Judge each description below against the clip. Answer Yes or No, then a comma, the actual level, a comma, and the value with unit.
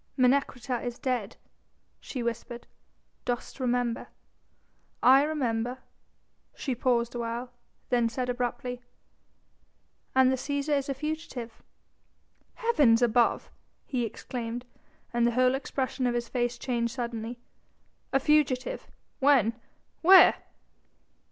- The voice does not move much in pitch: Yes, narrow, 2.1 semitones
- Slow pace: Yes, slow, 110 wpm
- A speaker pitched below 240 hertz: No, very high, 250 Hz